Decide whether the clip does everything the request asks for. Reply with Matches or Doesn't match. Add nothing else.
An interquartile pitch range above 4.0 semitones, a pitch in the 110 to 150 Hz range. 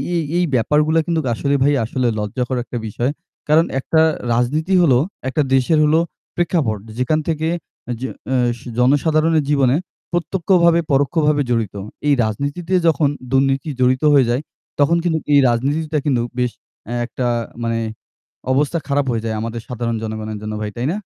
Matches